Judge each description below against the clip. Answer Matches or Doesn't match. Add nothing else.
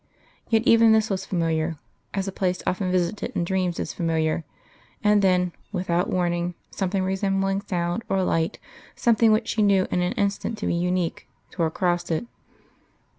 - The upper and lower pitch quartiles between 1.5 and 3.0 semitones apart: Matches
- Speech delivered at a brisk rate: Doesn't match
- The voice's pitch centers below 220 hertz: Matches